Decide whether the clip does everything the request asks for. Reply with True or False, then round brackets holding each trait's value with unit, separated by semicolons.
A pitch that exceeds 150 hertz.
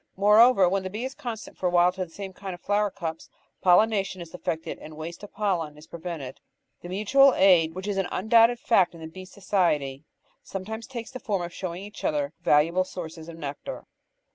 True (185 Hz)